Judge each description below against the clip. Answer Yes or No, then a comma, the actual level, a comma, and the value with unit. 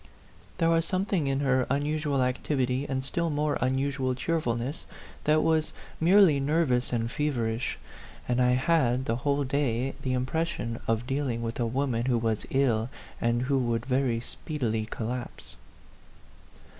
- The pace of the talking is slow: No, average, 145 wpm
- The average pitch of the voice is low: Yes, low, 130 Hz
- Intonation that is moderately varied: Yes, average, 3.5 semitones